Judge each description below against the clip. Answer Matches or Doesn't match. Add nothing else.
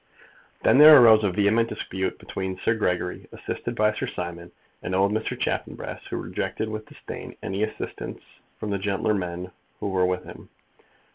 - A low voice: Matches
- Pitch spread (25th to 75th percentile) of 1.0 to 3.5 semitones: Matches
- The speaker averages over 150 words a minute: Matches